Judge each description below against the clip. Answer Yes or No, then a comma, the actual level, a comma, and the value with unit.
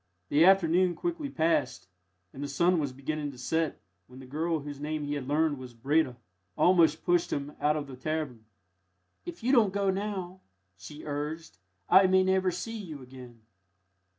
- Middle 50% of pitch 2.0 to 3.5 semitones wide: No, average, 4.7 semitones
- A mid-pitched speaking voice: Yes, medium, 155 Hz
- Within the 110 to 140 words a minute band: No, average, 175 wpm